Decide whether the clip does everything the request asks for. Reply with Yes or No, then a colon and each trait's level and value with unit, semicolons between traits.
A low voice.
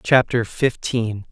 Yes: low, 120 Hz